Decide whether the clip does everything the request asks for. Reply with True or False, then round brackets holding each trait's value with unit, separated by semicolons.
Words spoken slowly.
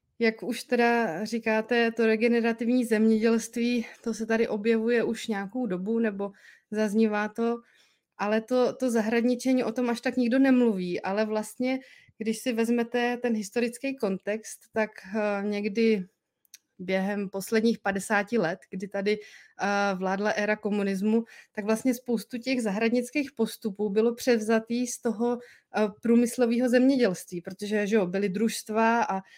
False (130 wpm)